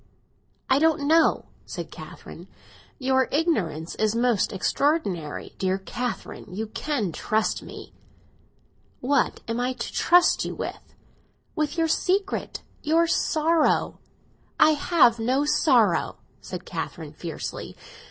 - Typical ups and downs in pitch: No, wide, 6.2 semitones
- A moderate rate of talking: No, slow, 115 wpm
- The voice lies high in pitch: Yes, very high, 265 Hz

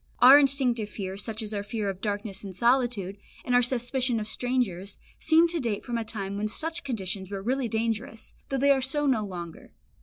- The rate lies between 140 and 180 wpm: No, fast, 205 wpm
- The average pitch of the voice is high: Yes, high, 225 Hz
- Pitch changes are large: No, average, 4.3 semitones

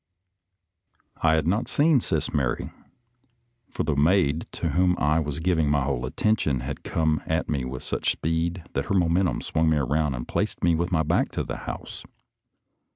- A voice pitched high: No, very low, 80 Hz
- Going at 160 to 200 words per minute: Yes, average, 180 wpm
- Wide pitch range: No, average, 3.3 semitones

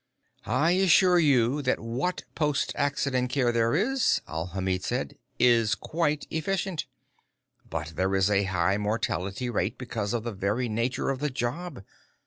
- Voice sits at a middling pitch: No, low, 120 Hz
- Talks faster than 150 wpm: No, average, 145 wpm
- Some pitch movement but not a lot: No, wide, 6.5 semitones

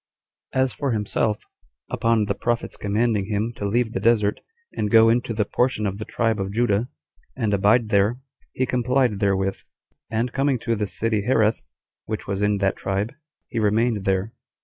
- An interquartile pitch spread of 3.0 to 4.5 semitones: No, narrow, 2.6 semitones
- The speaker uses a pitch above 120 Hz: No, low, 110 Hz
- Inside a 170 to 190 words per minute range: Yes, average, 180 wpm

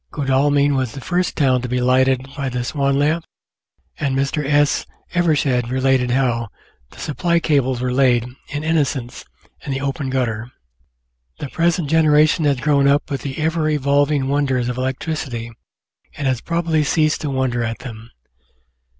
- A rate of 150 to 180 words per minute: Yes, average, 160 wpm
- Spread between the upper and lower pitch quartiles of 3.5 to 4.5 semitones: No, average, 2.7 semitones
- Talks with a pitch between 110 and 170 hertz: Yes, medium, 140 Hz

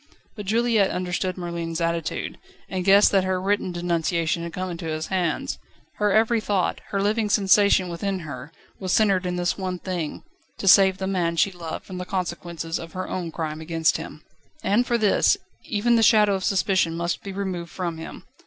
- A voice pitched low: No, medium, 185 Hz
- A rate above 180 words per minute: Yes, average, 190 wpm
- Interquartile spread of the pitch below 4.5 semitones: Yes, average, 2.7 semitones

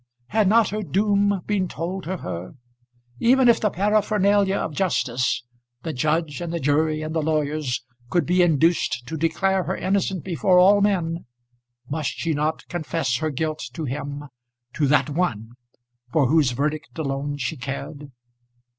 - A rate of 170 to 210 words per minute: No, average, 155 wpm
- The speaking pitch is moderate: Yes, medium, 160 Hz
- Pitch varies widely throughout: No, average, 4.6 semitones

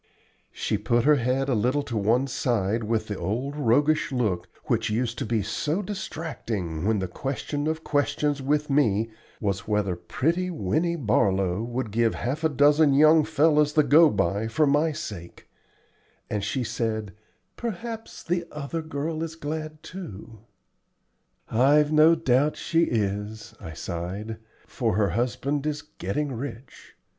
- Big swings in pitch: Yes, wide, 6.0 semitones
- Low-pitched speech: Yes, low, 130 Hz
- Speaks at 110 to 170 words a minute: Yes, average, 150 wpm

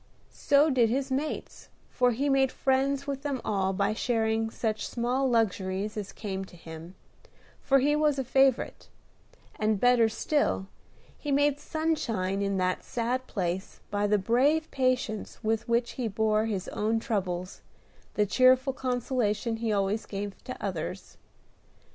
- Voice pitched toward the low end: No, high, 225 Hz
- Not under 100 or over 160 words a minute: Yes, average, 150 wpm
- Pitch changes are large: No, average, 4.6 semitones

